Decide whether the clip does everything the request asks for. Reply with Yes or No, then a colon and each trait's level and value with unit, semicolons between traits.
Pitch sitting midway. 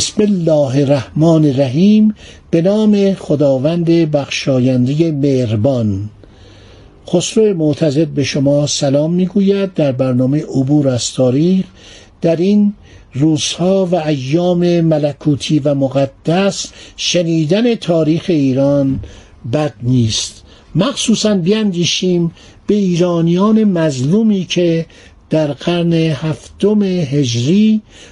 Yes: medium, 155 Hz